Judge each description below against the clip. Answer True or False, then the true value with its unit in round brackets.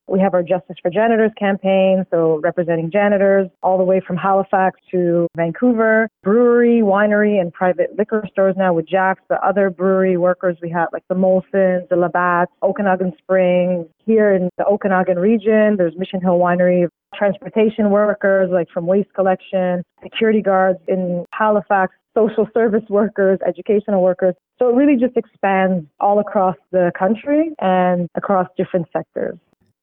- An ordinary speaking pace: True (155 wpm)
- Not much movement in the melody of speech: True (2.2 semitones)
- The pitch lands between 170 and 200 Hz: True (190 Hz)